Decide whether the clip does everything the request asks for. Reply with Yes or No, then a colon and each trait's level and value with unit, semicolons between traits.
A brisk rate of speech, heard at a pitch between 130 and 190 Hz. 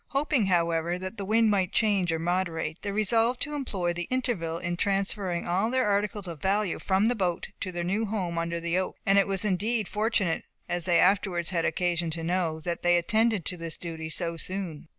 Yes: fast, 210 wpm; medium, 185 Hz